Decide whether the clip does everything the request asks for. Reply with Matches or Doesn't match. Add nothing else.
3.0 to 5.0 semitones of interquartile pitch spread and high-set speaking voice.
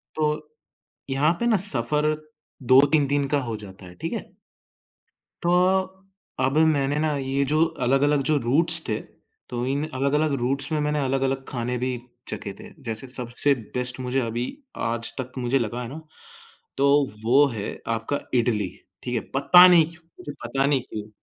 Doesn't match